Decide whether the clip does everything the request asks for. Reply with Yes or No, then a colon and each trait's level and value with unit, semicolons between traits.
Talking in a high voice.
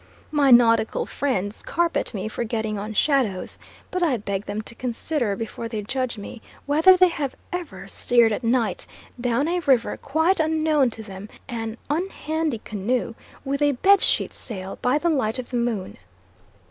Yes: high, 245 Hz